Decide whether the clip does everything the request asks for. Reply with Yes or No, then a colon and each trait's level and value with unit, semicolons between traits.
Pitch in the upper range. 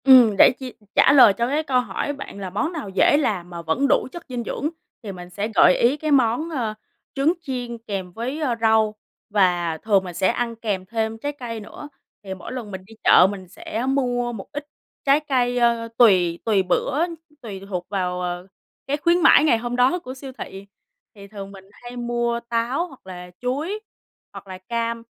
Yes: high, 230 Hz